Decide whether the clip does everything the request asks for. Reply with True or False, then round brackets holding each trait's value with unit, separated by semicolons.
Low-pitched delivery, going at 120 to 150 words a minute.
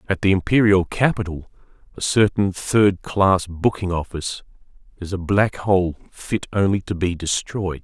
True (95 Hz; 145 wpm)